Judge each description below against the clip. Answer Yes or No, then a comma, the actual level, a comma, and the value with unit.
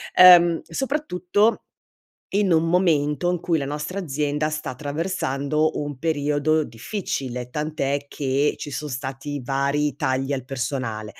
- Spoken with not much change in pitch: No, average, 3.3 semitones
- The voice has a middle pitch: Yes, medium, 150 Hz